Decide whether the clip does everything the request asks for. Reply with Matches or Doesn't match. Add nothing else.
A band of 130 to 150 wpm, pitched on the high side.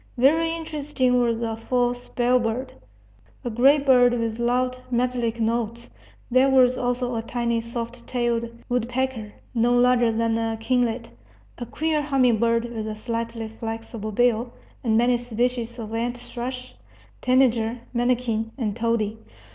Matches